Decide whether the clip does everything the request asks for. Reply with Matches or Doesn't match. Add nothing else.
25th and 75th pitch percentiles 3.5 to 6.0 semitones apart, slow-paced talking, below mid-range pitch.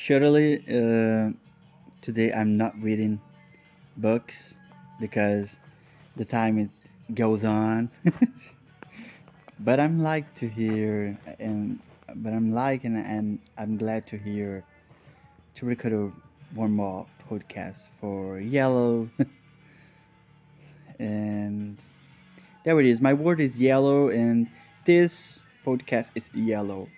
Matches